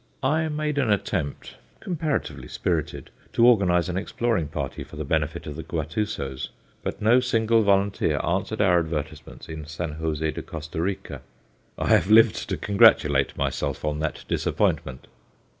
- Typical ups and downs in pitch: No, wide, 6.4 semitones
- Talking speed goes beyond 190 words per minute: No, average, 150 wpm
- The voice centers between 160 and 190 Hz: No, very low, 95 Hz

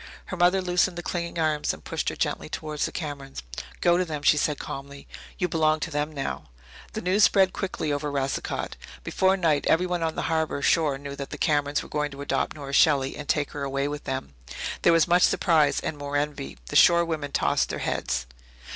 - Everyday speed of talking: No, fast, 210 wpm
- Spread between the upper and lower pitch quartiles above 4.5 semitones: No, average, 3.2 semitones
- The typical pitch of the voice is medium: Yes, medium, 150 Hz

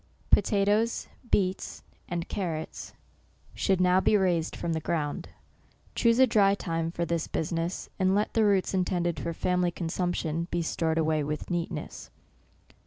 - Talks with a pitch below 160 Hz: No, medium, 175 Hz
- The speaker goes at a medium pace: Yes, average, 150 wpm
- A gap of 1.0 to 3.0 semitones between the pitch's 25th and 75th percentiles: Yes, narrow, 2.6 semitones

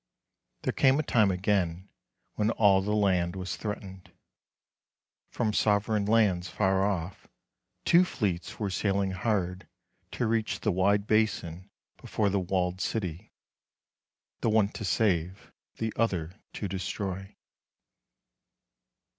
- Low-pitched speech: Yes, low, 100 Hz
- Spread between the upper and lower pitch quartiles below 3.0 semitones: Yes, narrow, 2.6 semitones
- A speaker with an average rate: No, slow, 120 wpm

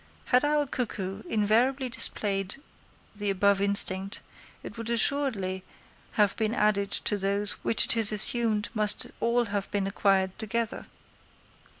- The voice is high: Yes, high, 210 Hz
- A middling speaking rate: No, slow, 130 wpm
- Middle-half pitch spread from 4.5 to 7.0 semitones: No, average, 2.7 semitones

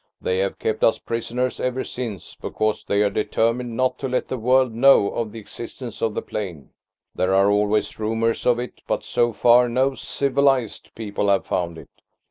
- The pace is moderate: Yes, average, 185 wpm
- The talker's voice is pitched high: No, low, 115 Hz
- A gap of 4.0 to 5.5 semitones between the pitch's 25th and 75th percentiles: No, average, 3.3 semitones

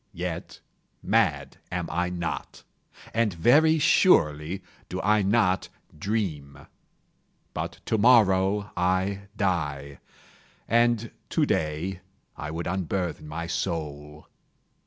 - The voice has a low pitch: Yes, very low, 90 Hz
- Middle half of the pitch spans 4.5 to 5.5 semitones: Yes, average, 4.9 semitones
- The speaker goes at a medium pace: No, slow, 95 wpm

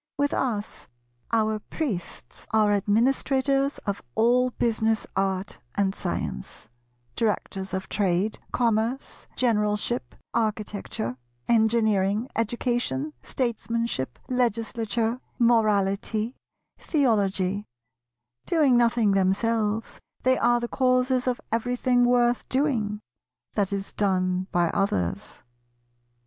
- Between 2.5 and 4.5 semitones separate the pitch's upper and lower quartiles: Yes, average, 3.4 semitones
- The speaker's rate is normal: No, slow, 90 wpm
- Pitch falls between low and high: No, high, 220 Hz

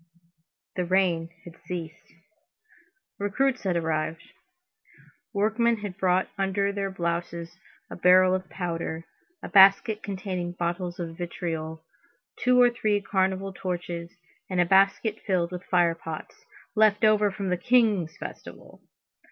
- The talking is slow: Yes, slow, 125 wpm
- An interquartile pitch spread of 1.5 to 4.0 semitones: Yes, average, 2.7 semitones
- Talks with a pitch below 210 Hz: Yes, medium, 185 Hz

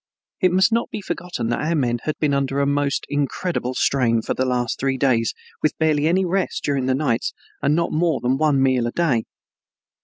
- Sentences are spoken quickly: Yes, fast, 210 wpm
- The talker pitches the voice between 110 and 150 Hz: Yes, medium, 140 Hz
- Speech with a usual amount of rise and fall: Yes, average, 3.9 semitones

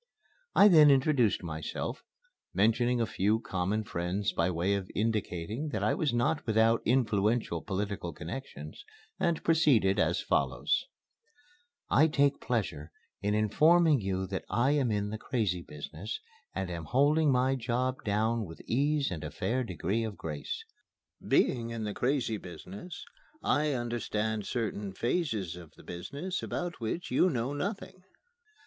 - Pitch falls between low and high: No, low, 110 Hz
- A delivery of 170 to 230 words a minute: No, average, 145 wpm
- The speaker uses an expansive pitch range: Yes, wide, 5.9 semitones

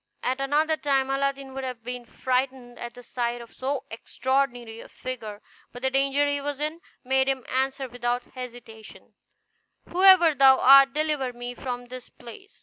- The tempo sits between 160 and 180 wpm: Yes, average, 165 wpm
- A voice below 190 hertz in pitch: No, very high, 265 Hz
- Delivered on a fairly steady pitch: Yes, narrow, 2.1 semitones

